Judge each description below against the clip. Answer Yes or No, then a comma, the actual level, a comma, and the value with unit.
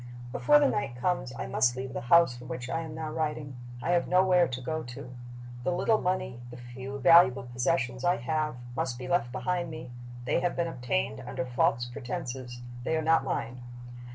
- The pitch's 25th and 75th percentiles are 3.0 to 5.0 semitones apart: No, wide, 5.4 semitones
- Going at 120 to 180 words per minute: No, average, 195 wpm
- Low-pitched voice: Yes, low, 130 Hz